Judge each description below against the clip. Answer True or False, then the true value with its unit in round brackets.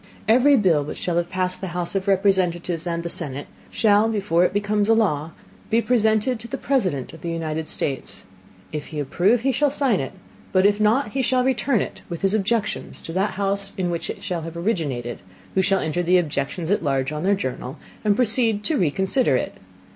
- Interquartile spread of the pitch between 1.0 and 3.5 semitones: False (4.7 semitones)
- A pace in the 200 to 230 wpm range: True (205 wpm)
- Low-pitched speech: False (190 Hz)